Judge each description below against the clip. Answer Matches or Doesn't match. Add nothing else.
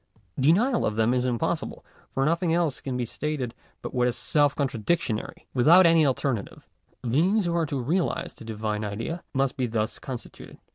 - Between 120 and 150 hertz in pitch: Matches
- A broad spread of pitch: Matches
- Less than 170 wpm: Doesn't match